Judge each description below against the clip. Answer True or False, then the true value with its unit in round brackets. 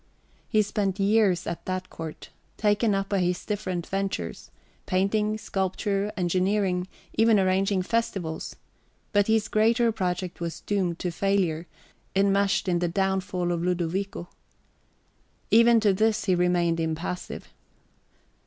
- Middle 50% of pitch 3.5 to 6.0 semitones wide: False (2.6 semitones)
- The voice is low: False (190 Hz)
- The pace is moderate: False (125 wpm)